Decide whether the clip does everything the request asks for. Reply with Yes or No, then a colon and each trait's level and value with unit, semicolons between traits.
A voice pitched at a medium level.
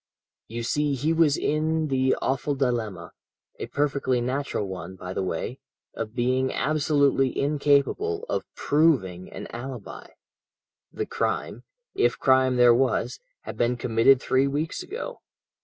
No: low, 130 Hz